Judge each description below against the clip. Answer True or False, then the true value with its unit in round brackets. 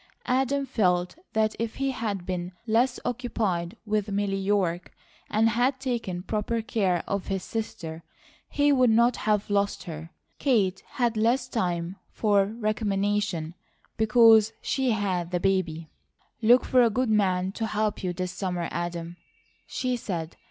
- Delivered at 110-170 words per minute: True (145 wpm)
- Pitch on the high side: True (210 Hz)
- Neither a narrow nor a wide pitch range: True (4.2 semitones)